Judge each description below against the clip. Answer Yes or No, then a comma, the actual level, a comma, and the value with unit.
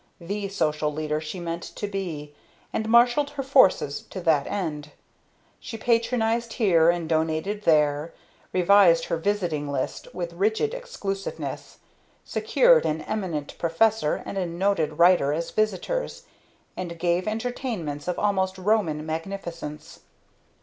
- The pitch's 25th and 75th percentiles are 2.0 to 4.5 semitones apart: No, average, 5.2 semitones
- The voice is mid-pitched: Yes, medium, 180 Hz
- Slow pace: Yes, slow, 130 wpm